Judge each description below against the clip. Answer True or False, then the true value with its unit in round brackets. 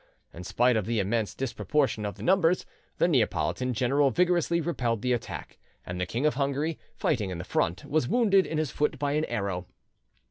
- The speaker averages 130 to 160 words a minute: False (190 wpm)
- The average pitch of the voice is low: True (125 Hz)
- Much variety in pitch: True (6.8 semitones)